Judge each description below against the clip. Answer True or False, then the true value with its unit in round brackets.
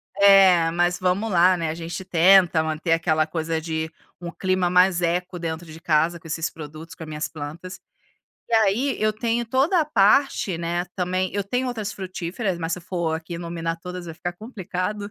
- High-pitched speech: False (175 Hz)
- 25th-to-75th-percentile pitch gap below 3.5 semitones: True (2.9 semitones)